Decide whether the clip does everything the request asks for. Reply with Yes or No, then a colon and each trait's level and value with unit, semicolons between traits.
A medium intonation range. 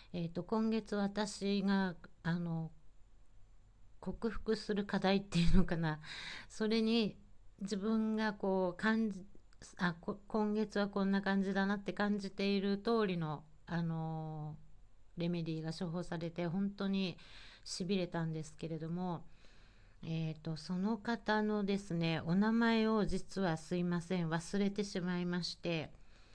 Yes: average, 3.8 semitones